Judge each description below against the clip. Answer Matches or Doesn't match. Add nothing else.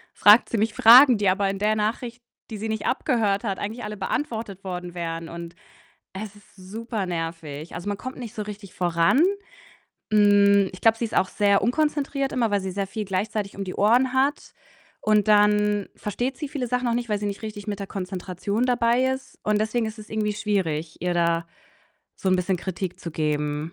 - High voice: Matches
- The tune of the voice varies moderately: Matches